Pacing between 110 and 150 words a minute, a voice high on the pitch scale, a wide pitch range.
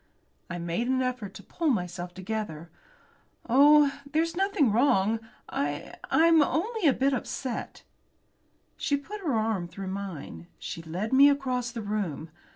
Yes: average, 145 wpm; high, 230 Hz; wide, 7.4 semitones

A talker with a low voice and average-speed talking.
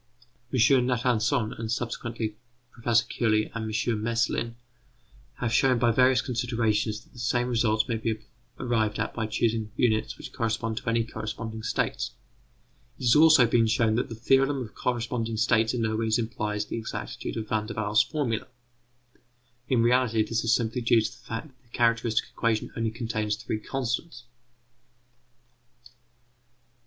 Yes: low, 115 Hz; average, 155 wpm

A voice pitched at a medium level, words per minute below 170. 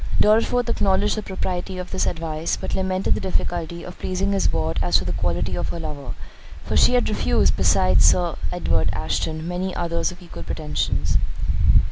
No: medium, 170 Hz; average, 175 wpm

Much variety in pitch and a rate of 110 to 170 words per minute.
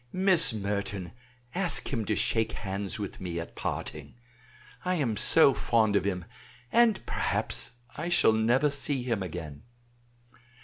Yes: wide, 6.4 semitones; average, 140 wpm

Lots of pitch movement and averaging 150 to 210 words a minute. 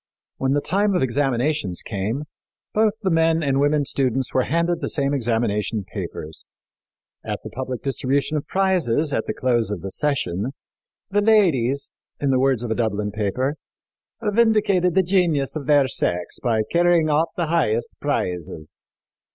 Yes: wide, 6.0 semitones; average, 160 wpm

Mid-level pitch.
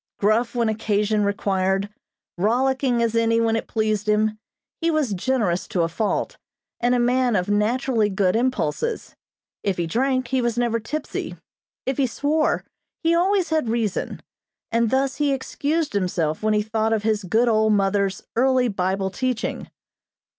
No: high, 225 Hz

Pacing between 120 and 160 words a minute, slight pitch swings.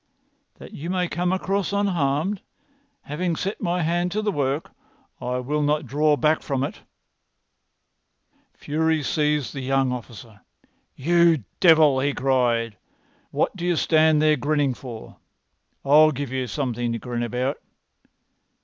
No: average, 140 wpm; average, 4.3 semitones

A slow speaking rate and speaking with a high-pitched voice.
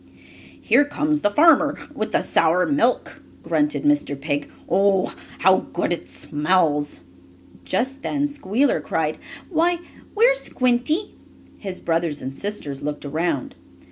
Yes: slow, 125 wpm; high, 205 Hz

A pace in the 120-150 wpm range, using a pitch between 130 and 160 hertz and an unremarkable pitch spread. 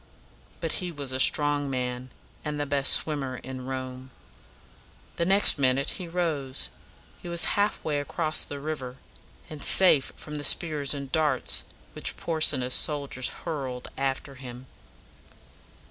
Yes: average, 140 wpm; medium, 140 Hz; average, 3.1 semitones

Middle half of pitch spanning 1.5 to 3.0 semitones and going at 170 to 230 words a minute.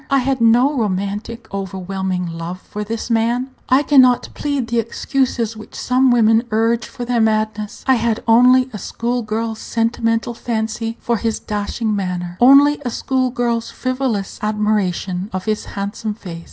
No: average, 2.7 semitones; average, 160 wpm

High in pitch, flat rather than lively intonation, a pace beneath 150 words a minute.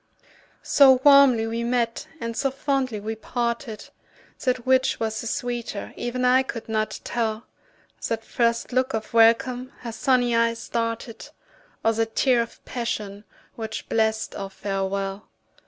Yes: high, 230 Hz; narrow, 2.1 semitones; average, 140 wpm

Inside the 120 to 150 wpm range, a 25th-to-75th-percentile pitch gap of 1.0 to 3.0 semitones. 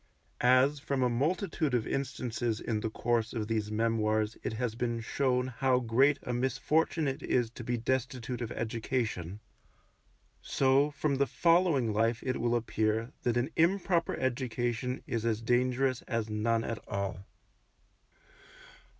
Yes: average, 145 wpm; average, 2.7 semitones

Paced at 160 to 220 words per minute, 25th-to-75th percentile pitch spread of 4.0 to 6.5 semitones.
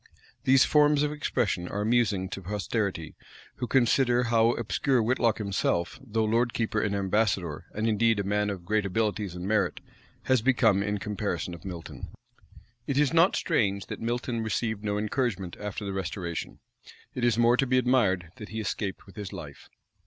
No: average, 175 wpm; average, 3.5 semitones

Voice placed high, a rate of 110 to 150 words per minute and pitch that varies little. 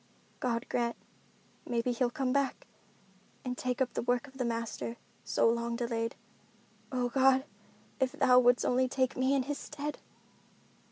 Yes: very high, 250 Hz; average, 145 wpm; narrow, 1.8 semitones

